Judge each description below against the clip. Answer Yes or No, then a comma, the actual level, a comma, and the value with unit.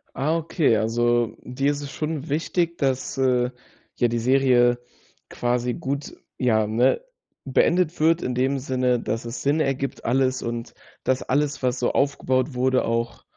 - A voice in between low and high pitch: No, low, 130 Hz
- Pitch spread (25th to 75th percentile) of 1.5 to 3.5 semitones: Yes, narrow, 2.6 semitones